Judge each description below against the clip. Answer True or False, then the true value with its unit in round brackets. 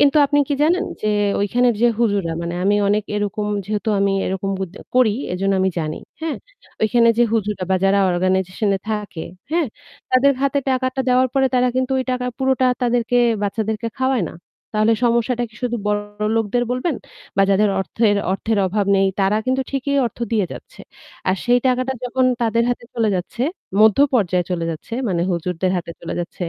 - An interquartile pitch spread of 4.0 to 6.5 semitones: True (4.4 semitones)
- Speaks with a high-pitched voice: True (220 Hz)